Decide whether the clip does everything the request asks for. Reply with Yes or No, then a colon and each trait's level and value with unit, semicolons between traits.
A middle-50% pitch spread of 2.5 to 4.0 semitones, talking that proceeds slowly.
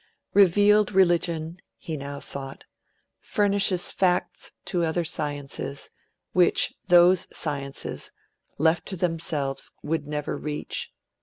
Yes: average, 3.6 semitones; slow, 100 wpm